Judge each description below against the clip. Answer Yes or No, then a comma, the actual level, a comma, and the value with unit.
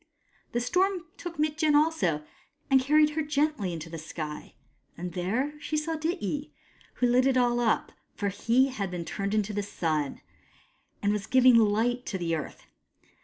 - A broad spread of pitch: Yes, wide, 7.7 semitones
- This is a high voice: Yes, high, 240 Hz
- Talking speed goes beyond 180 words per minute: No, average, 170 wpm